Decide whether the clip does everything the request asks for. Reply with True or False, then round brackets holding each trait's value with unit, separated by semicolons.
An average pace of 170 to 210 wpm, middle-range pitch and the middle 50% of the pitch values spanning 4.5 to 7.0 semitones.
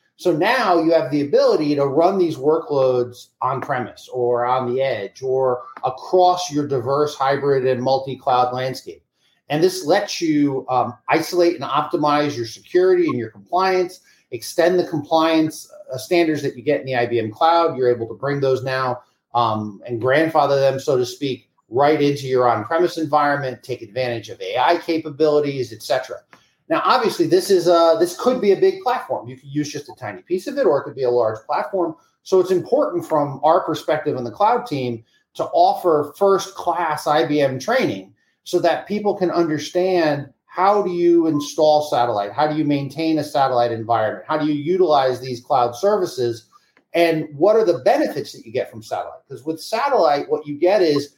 True (180 wpm; 150 Hz; 5.0 semitones)